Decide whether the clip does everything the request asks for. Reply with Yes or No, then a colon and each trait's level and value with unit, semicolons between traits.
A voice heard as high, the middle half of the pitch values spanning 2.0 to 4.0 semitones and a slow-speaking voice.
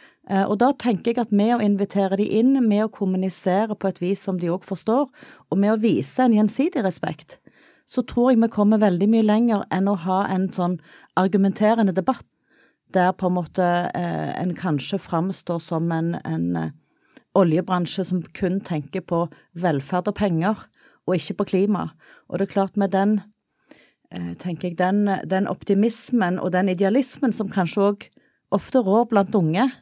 No: high, 195 Hz; average, 2.9 semitones; average, 170 wpm